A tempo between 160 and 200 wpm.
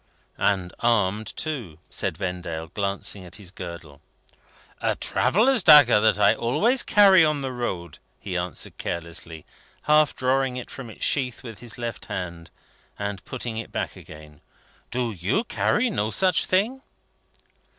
No: average, 145 wpm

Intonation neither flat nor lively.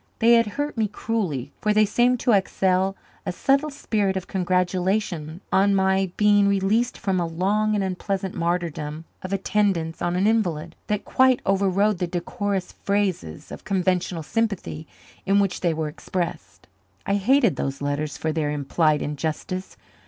Yes: average, 3.7 semitones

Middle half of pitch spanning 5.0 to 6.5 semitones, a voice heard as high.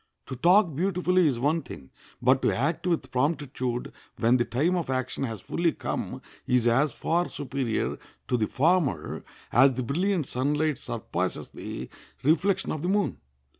No: average, 5.3 semitones; medium, 145 Hz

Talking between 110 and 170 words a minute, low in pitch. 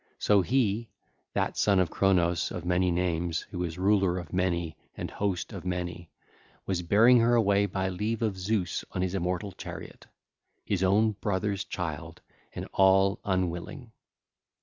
Yes: average, 150 wpm; very low, 95 Hz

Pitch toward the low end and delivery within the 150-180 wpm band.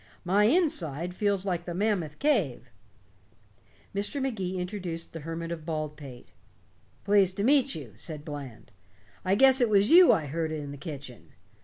No: medium, 175 Hz; average, 155 wpm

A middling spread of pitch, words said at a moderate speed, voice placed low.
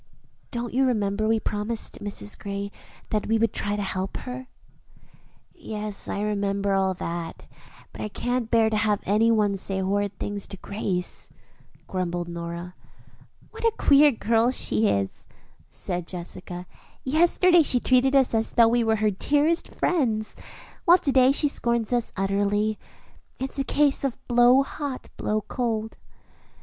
No: average, 4.0 semitones; average, 155 wpm; high, 215 Hz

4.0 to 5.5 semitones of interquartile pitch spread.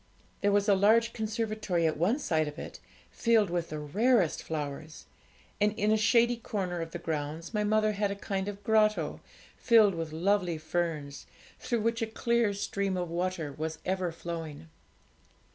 Yes: average, 4.8 semitones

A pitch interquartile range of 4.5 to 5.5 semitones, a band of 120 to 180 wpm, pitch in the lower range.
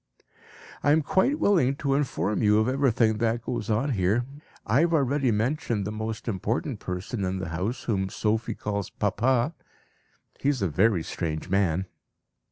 Yes: average, 5.1 semitones; average, 165 wpm; low, 110 Hz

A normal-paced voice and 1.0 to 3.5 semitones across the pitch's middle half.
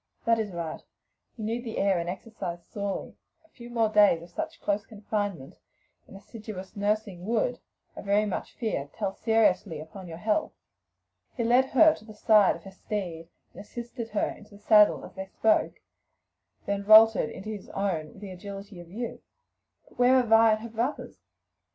Yes: average, 180 wpm; average, 2.8 semitones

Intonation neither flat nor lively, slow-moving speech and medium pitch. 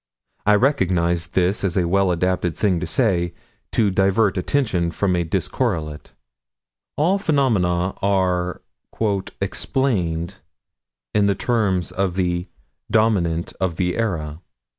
No: average, 3.1 semitones; slow, 120 wpm; very low, 95 Hz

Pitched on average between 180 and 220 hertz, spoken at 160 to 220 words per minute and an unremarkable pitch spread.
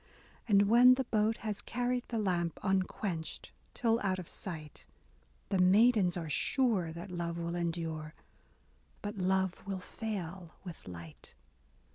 No: medium, 185 Hz; average, 140 wpm; average, 4.1 semitones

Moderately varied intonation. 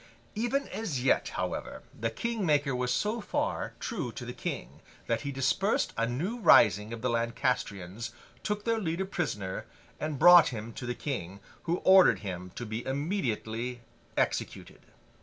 No: wide, 8.7 semitones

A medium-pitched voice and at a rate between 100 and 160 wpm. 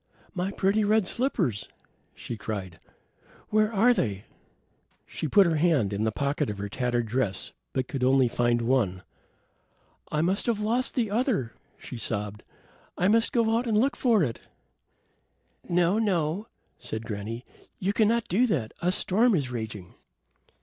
Yes: medium, 155 Hz; average, 155 wpm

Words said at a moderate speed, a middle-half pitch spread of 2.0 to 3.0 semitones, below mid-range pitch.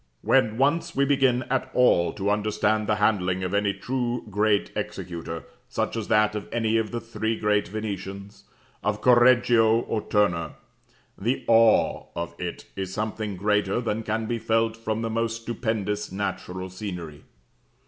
Yes: average, 155 wpm; narrow, 2.4 semitones; low, 110 Hz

